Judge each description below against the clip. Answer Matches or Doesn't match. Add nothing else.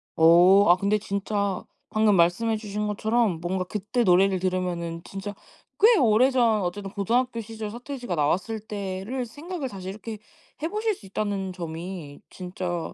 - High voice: Matches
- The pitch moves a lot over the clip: Doesn't match